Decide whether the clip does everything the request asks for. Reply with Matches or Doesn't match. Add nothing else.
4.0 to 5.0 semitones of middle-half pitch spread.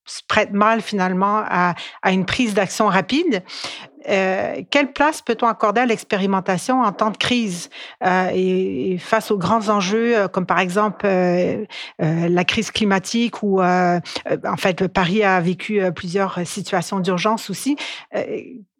Doesn't match